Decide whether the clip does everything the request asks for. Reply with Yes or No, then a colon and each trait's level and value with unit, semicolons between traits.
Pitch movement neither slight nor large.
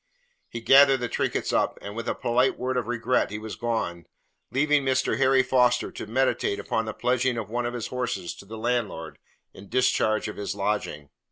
Yes: average, 3.3 semitones